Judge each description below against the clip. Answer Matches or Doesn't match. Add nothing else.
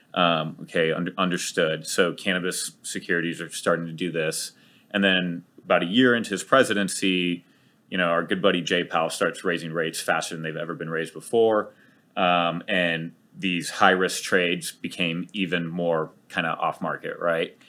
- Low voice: Matches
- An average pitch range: Doesn't match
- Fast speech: Doesn't match